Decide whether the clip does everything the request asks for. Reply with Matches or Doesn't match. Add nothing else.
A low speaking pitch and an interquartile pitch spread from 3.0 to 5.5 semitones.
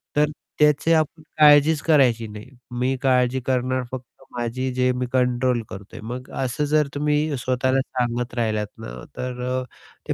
Doesn't match